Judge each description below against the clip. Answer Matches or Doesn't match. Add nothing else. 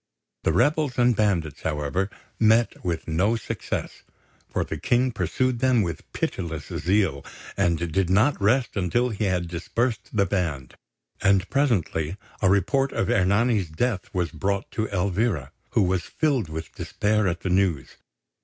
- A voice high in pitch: Doesn't match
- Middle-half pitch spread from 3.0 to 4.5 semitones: Doesn't match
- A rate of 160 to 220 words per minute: Doesn't match